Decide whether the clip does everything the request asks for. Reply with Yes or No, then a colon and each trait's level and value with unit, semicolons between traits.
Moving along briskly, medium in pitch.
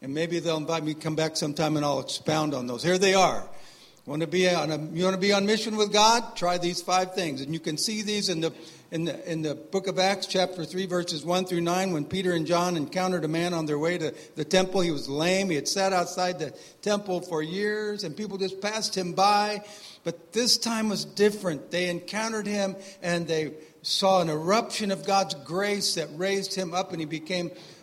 Yes: fast, 230 wpm; medium, 180 Hz